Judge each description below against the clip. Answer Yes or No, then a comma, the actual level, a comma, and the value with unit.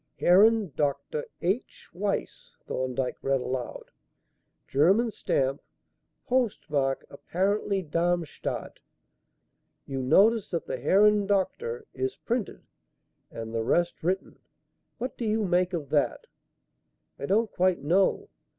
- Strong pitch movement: Yes, wide, 6.9 semitones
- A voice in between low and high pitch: Yes, medium, 180 Hz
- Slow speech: Yes, slow, 110 wpm